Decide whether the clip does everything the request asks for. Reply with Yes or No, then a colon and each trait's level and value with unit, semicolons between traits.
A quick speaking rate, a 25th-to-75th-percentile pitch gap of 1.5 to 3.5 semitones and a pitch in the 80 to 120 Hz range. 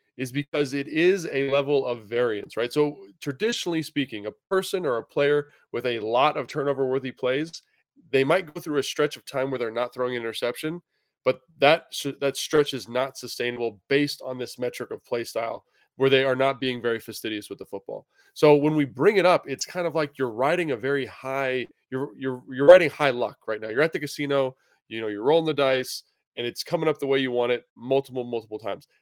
No: fast, 220 wpm; average, 3.1 semitones; low, 135 Hz